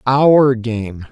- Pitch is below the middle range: Yes, low, 125 Hz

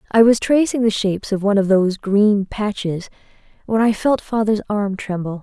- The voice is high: Yes, high, 205 Hz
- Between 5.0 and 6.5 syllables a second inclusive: Yes, 5.2 syllables/s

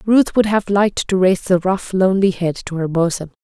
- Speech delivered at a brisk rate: Yes, fast, 225 wpm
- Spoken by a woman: Yes, female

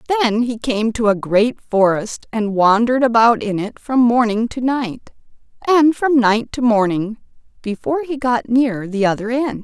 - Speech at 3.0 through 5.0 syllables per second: Yes, 4.5 syllables/s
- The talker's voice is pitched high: Yes, high, 235 Hz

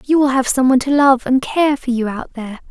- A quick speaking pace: Yes, fast, 290 wpm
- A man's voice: No, female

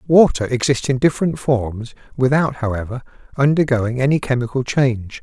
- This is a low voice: Yes, low, 130 Hz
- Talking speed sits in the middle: No, slow, 125 wpm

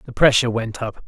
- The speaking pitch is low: Yes, low, 115 Hz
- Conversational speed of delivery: No, fast, 225 wpm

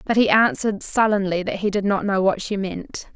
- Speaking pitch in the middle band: No, high, 200 Hz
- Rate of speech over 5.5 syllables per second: No, 5.3 syllables/s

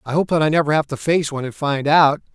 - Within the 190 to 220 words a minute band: No, fast, 305 wpm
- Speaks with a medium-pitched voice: Yes, medium, 150 Hz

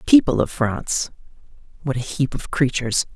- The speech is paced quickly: No, average, 150 wpm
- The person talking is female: Yes, female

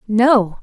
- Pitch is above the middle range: Yes, high, 225 Hz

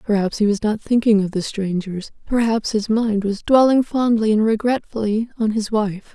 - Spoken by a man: No, female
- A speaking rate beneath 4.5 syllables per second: No, 5.1 syllables/s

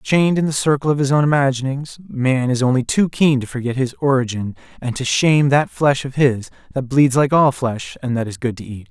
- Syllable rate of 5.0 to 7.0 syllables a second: Yes, 5.5 syllables/s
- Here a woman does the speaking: No, male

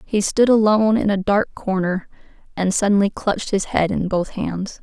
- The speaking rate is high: No, average, 185 wpm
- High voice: Yes, high, 200 Hz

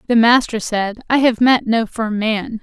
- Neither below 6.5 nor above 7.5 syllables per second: No, 4.2 syllables/s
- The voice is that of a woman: Yes, female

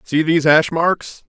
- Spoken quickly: No, average, 175 wpm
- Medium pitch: Yes, medium, 160 Hz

